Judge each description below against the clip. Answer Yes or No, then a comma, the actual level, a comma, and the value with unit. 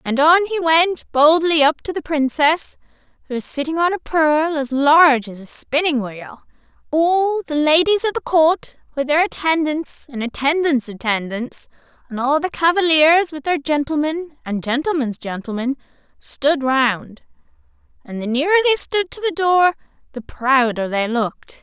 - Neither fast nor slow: Yes, average, 160 wpm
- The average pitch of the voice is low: No, very high, 295 Hz